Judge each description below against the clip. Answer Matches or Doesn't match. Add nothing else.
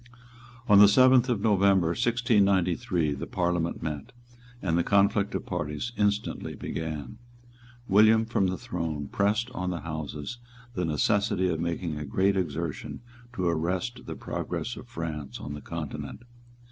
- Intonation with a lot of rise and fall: Doesn't match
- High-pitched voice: Doesn't match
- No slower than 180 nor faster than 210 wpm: Doesn't match